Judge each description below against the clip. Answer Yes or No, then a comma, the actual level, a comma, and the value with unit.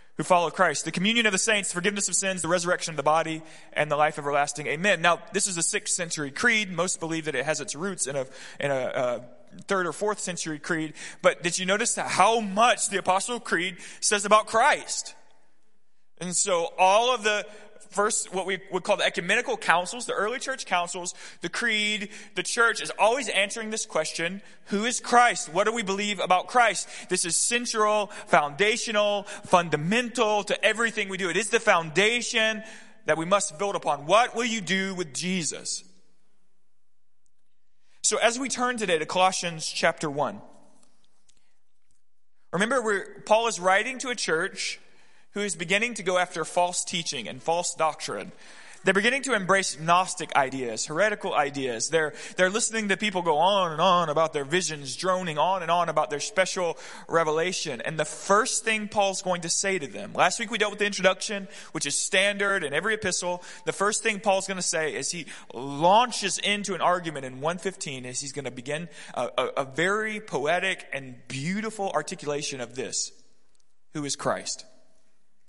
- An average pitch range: Yes, average, 4.3 semitones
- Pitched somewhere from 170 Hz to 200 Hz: Yes, high, 190 Hz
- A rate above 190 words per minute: No, average, 180 wpm